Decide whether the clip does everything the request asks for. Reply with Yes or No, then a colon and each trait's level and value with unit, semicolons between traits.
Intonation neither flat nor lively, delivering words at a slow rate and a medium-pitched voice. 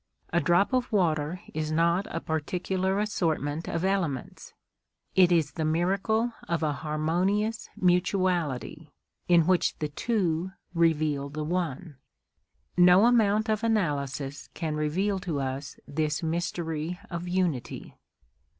Yes: average, 3.6 semitones; slow, 125 wpm; medium, 170 Hz